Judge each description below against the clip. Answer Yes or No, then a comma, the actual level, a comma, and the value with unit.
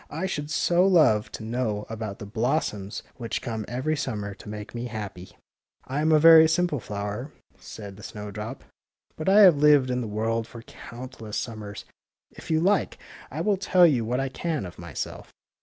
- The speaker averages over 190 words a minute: Yes, average, 200 wpm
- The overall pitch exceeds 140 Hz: No, low, 120 Hz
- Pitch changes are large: Yes, wide, 6.5 semitones